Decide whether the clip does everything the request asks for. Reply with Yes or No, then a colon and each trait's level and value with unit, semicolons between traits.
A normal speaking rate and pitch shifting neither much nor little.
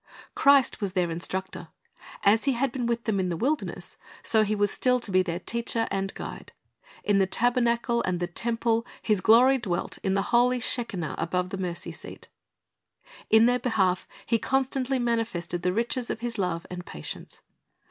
Yes: average, 180 wpm; average, 4.6 semitones